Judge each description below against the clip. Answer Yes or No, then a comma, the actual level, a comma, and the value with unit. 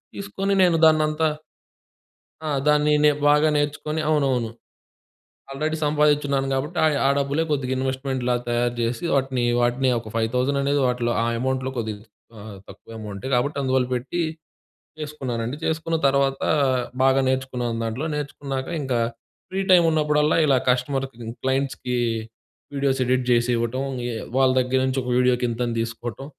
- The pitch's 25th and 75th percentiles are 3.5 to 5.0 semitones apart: No, average, 3.1 semitones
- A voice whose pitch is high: No, low, 130 Hz